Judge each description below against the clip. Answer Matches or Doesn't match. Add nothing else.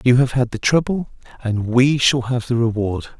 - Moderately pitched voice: Doesn't match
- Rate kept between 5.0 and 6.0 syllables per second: Doesn't match